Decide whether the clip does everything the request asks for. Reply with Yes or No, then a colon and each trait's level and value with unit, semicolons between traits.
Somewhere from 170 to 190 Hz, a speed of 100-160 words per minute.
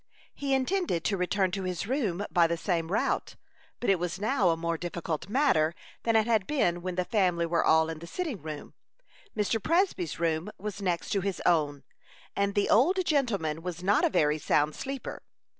No: medium, 185 Hz; average, 190 wpm